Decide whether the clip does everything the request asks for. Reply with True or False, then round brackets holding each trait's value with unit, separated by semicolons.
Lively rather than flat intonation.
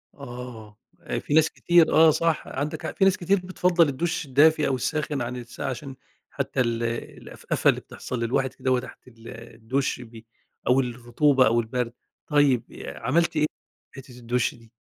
False (4.1 semitones)